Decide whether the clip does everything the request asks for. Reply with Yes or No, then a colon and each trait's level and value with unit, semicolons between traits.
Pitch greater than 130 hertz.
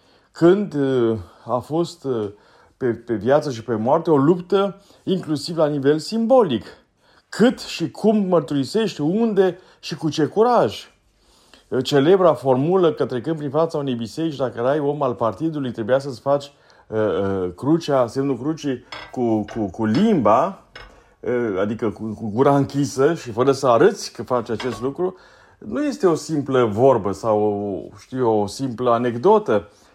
Yes: medium, 140 Hz